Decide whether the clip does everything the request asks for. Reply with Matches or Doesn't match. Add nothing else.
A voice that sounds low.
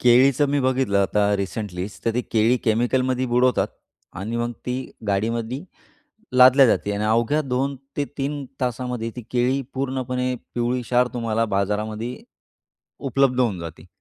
Matches